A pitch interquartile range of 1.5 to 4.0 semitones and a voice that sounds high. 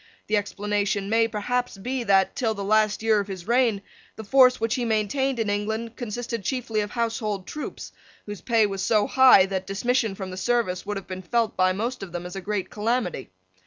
Yes: average, 3.0 semitones; high, 215 Hz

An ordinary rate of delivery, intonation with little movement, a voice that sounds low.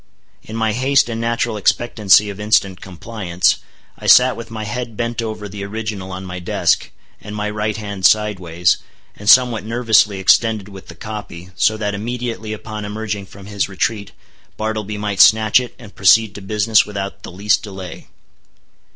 Yes: average, 170 wpm; narrow, 2.1 semitones; low, 105 Hz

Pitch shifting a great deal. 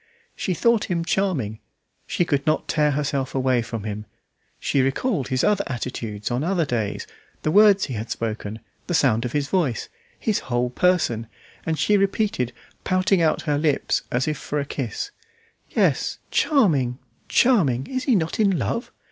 Yes: wide, 7.2 semitones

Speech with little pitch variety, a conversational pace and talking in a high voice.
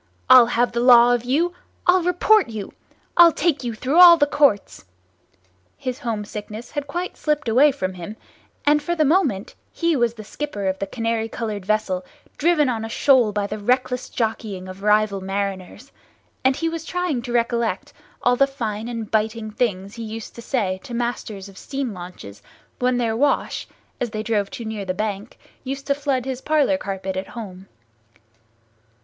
No: average, 4.9 semitones; average, 180 wpm; high, 235 Hz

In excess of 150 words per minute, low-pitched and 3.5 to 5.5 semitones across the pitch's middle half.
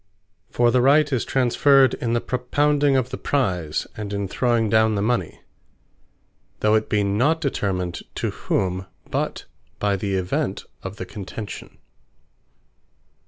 No: average, 140 wpm; low, 110 Hz; average, 4.6 semitones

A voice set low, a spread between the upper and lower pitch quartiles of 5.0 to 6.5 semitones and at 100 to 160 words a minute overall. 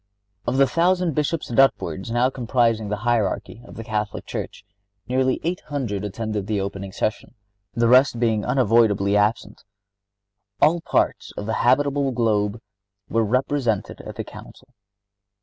No: low, 115 Hz; average, 4.0 semitones; average, 145 wpm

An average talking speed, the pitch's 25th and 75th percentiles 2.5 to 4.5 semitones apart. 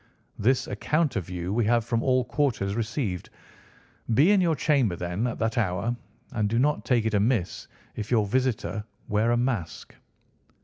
Yes: average, 170 wpm; average, 3.9 semitones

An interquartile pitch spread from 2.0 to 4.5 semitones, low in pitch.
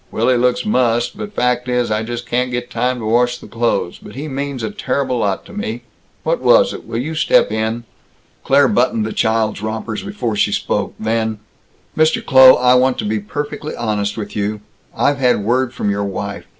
Yes: average, 2.9 semitones; low, 120 Hz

